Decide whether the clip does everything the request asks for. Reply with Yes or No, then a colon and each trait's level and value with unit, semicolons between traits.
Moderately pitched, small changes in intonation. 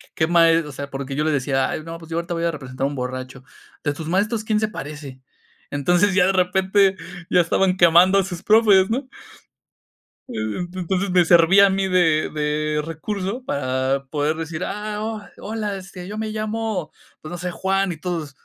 No: medium, 175 Hz; average, 4.4 semitones